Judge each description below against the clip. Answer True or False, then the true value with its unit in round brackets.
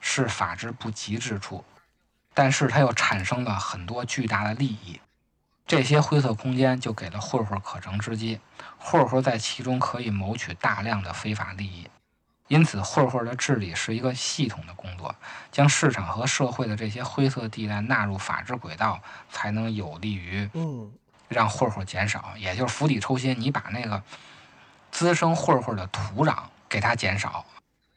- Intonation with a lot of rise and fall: False (4.4 semitones)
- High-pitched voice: False (110 Hz)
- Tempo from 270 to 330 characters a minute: False (255 characters per minute)